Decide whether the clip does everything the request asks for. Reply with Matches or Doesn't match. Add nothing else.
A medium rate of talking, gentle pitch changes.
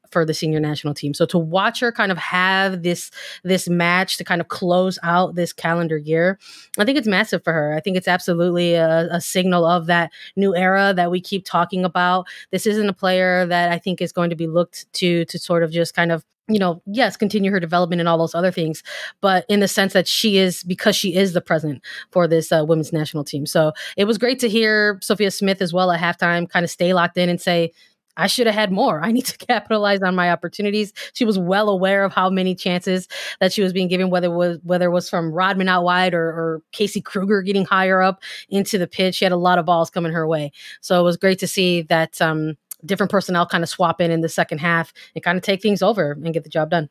Doesn't match